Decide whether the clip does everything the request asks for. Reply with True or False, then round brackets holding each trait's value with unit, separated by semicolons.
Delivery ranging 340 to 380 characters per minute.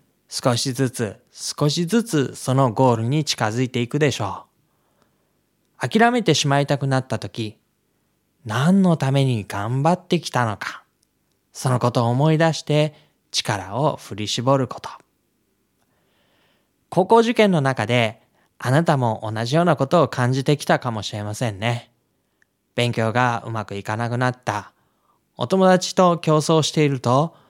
False (270 characters per minute)